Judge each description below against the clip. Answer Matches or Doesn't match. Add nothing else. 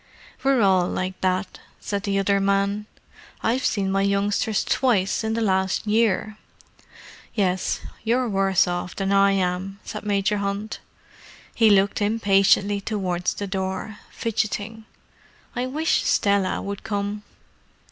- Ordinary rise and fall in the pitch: Doesn't match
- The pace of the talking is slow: Matches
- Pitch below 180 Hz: Doesn't match